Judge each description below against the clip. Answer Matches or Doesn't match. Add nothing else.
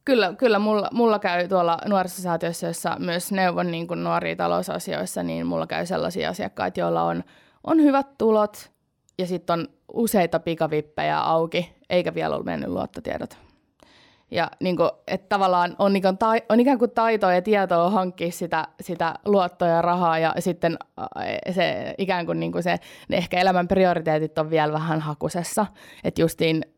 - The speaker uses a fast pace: Matches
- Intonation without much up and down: Doesn't match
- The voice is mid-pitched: Matches